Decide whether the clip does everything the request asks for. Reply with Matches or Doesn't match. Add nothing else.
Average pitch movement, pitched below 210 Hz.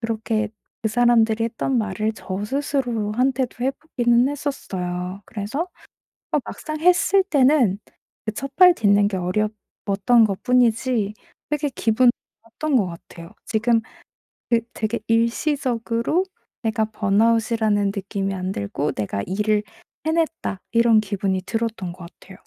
Doesn't match